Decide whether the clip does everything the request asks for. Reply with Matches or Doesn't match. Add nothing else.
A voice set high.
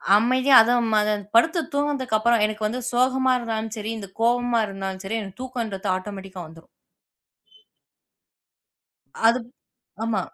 Matches